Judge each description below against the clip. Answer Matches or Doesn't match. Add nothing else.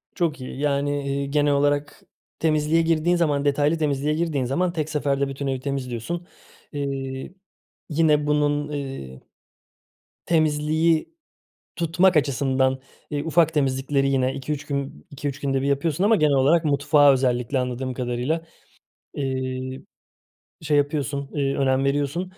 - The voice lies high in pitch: Doesn't match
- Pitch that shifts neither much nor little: Doesn't match